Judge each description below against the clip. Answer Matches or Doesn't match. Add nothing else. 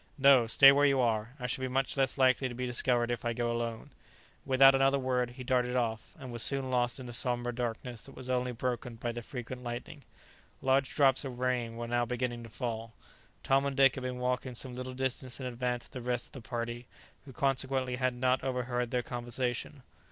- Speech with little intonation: Matches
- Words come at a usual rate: Doesn't match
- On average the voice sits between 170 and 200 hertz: Doesn't match